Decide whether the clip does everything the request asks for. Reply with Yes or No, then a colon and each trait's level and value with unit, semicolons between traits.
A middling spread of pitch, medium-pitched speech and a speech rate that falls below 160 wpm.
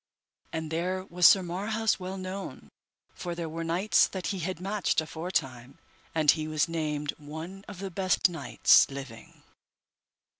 Yes: average, 3.3 semitones; medium, 170 Hz; average, 150 wpm